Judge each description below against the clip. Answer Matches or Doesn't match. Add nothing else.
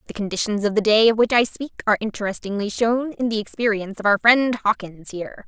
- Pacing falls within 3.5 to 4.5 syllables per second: Doesn't match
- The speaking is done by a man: Doesn't match